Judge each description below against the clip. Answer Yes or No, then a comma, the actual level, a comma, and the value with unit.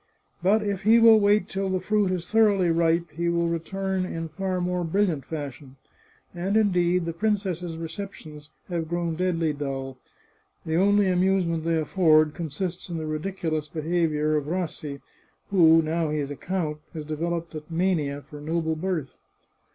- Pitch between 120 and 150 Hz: No, medium, 170 Hz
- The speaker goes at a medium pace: Yes, average, 160 wpm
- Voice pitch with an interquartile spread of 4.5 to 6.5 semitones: No, average, 3.2 semitones